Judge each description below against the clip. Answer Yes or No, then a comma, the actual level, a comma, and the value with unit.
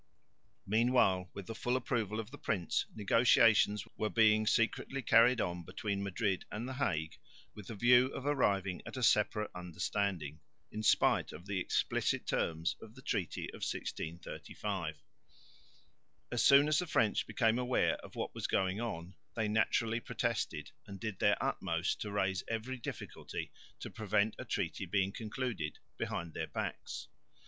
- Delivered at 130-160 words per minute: Yes, average, 155 wpm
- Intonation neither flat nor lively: Yes, average, 3.8 semitones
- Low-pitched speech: Yes, low, 105 Hz